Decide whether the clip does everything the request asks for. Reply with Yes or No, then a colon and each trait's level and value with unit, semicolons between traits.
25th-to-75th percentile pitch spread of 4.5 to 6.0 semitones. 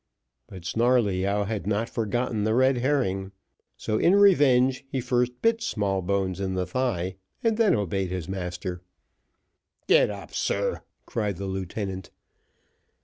Yes: average, 4.8 semitones